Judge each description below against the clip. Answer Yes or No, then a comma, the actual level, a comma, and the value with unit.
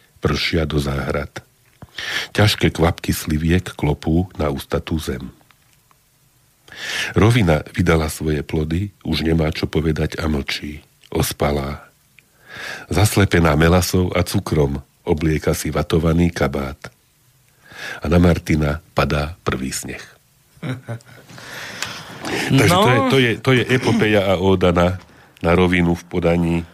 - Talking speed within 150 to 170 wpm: No, slow, 110 wpm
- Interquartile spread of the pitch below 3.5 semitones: No, average, 4.4 semitones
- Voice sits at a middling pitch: No, very low, 85 Hz